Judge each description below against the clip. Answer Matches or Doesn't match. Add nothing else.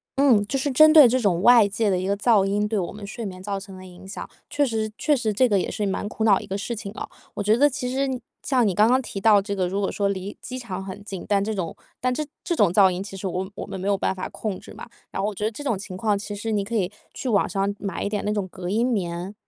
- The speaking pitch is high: Matches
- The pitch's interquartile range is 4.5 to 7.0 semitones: Doesn't match